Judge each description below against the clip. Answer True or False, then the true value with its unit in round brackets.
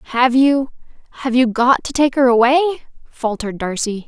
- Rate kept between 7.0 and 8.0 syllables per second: False (5.3 syllables/s)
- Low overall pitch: False (250 Hz)